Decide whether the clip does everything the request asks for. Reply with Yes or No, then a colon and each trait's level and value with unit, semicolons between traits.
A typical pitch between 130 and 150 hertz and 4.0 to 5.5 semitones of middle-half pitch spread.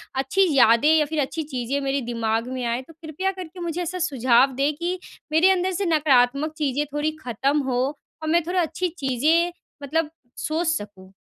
No: very high, 300 Hz; average, 4.4 semitones